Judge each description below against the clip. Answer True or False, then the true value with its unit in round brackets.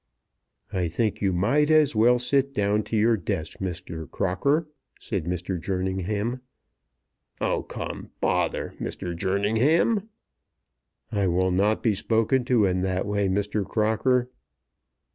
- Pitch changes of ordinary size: True (4.6 semitones)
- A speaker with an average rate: False (125 wpm)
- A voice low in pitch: True (105 Hz)